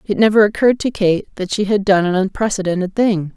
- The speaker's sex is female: Yes, female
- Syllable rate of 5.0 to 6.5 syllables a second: Yes, 6.0 syllables/s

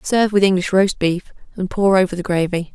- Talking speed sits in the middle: No, fast, 220 wpm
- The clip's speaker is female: Yes, female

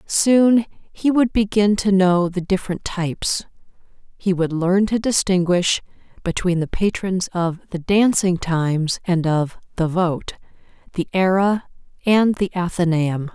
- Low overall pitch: No, medium, 185 Hz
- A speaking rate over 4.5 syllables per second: No, 4.0 syllables/s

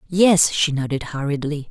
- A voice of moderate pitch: Yes, medium, 155 Hz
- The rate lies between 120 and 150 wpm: Yes, average, 140 wpm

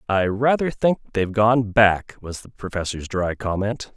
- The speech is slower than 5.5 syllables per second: Yes, 4.5 syllables/s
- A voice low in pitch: Yes, low, 105 Hz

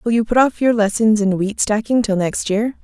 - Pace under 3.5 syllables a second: No, 5.2 syllables/s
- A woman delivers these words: Yes, female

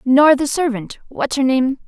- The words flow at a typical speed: Yes, average, 160 wpm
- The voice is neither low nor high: No, very high, 270 Hz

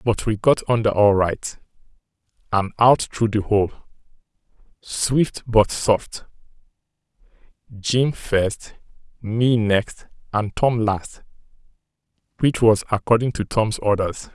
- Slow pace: Yes, slow, 115 wpm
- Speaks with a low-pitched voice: Yes, low, 110 Hz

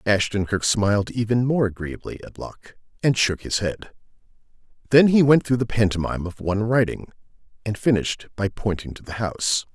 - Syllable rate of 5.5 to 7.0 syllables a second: Yes, 5.6 syllables/s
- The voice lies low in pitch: Yes, low, 110 Hz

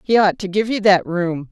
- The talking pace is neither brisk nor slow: No, fast, 280 wpm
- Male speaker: No, female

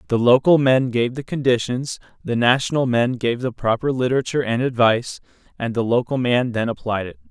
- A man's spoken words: Yes, male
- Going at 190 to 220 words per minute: No, average, 180 wpm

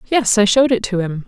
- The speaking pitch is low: No, high, 215 Hz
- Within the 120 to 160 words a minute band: No, fast, 280 wpm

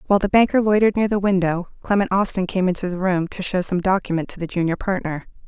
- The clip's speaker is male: No, female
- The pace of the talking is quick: Yes, fast, 230 wpm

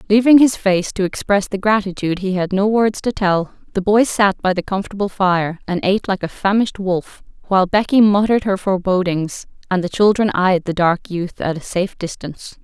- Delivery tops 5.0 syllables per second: Yes, 5.5 syllables/s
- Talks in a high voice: Yes, high, 195 Hz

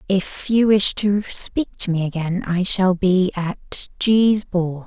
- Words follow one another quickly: No, average, 175 wpm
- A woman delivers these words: Yes, female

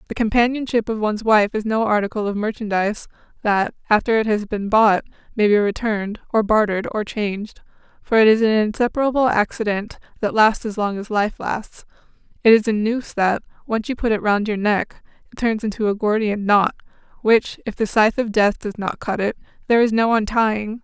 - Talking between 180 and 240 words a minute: Yes, average, 195 wpm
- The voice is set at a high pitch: Yes, high, 215 Hz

